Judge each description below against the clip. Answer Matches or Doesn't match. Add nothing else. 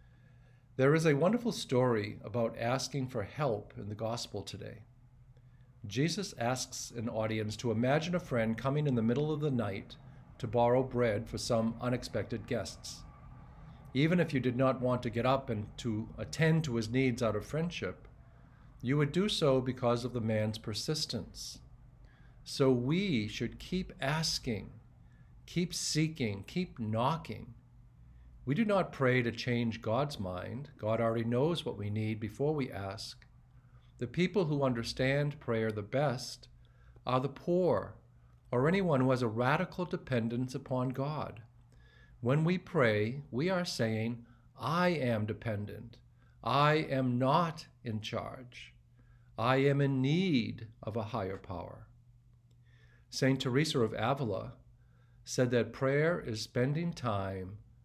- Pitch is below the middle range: Matches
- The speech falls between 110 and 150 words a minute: Matches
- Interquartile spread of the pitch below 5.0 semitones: Matches